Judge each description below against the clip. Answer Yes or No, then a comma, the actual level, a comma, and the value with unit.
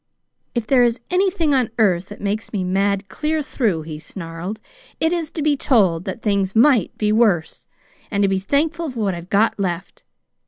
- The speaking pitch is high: Yes, high, 210 Hz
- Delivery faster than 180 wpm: Yes, average, 190 wpm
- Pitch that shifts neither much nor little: No, wide, 6.2 semitones